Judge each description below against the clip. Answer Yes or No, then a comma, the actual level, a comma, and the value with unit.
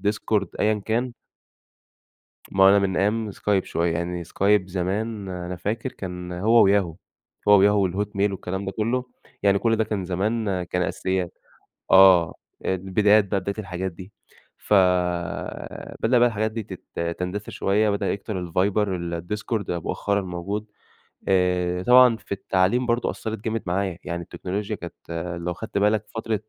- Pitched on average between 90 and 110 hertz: Yes, low, 100 Hz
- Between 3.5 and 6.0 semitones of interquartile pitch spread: No, average, 2.8 semitones